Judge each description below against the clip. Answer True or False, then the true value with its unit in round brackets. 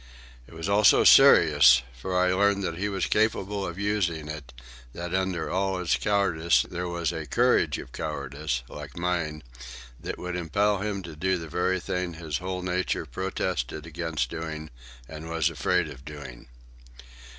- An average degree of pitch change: True (3.4 semitones)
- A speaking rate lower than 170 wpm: True (160 wpm)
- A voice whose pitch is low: True (85 Hz)